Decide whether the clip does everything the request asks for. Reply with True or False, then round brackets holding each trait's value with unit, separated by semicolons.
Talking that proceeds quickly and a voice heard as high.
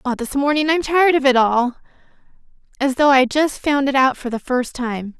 True (220 wpm; 265 Hz)